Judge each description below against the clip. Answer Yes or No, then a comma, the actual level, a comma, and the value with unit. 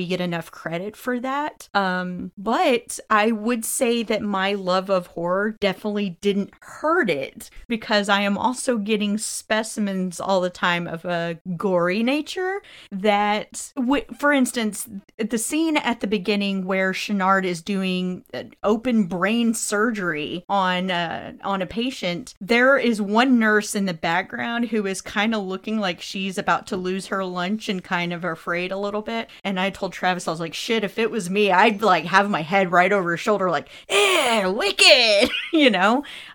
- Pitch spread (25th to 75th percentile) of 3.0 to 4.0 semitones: Yes, average, 3.6 semitones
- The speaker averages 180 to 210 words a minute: No, average, 170 wpm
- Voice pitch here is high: Yes, high, 205 Hz